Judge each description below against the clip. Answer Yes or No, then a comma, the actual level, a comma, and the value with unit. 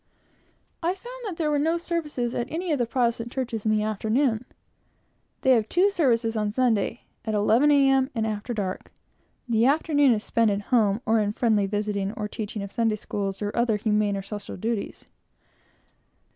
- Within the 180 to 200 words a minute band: Yes, average, 185 wpm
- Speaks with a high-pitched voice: Yes, high, 230 Hz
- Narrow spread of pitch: No, average, 4.2 semitones